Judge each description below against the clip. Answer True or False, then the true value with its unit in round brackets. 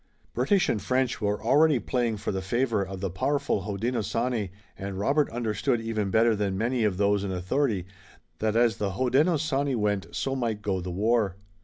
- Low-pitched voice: True (110 Hz)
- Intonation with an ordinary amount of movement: True (4.2 semitones)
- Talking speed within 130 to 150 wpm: False (175 wpm)